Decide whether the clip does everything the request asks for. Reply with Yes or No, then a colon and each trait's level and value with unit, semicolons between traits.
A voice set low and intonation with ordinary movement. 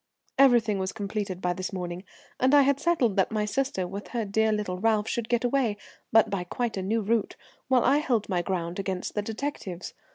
No: high, 210 Hz; average, 4.1 semitones